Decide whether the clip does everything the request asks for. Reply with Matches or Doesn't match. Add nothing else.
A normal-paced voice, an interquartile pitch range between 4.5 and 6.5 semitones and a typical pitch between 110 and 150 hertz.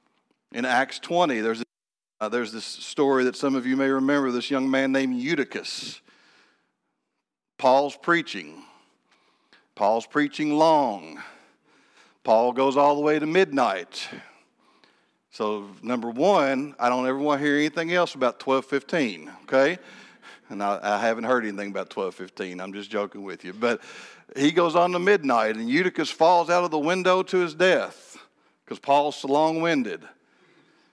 Matches